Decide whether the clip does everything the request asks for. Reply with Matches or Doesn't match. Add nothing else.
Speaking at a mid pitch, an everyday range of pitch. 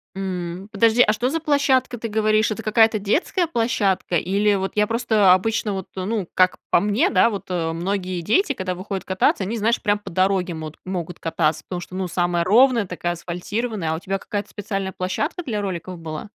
Doesn't match